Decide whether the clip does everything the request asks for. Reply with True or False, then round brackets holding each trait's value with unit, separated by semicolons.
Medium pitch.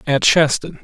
True (145 Hz)